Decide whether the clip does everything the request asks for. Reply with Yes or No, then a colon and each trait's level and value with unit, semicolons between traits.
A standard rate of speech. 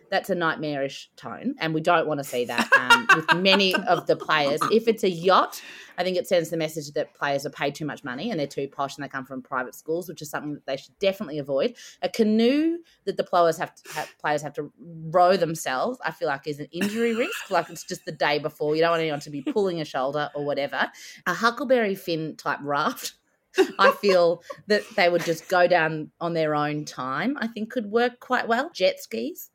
No: fast, 230 wpm